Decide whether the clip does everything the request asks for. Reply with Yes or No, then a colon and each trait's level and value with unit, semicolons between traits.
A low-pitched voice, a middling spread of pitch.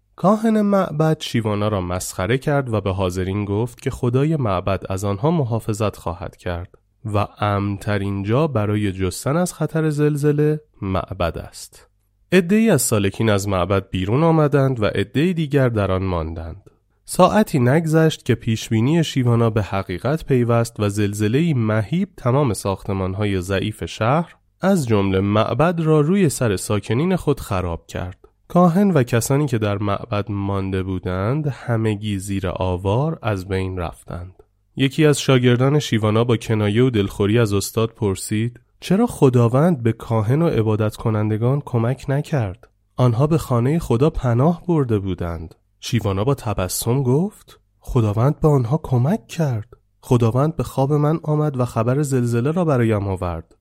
No: low, 115 Hz; wide, 6.5 semitones